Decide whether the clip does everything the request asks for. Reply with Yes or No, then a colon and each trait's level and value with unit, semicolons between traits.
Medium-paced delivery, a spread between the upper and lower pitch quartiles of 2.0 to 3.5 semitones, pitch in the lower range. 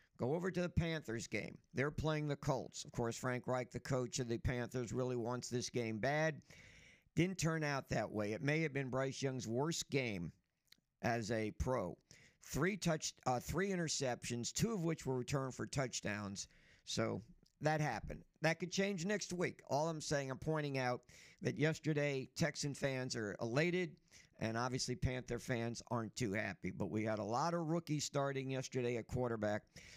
No: average, 180 wpm; average, 4.6 semitones; low, 130 Hz